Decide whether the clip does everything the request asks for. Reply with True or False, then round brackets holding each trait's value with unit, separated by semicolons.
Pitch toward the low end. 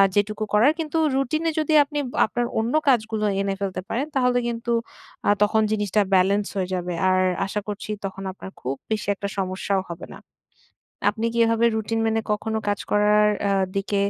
False (210 Hz)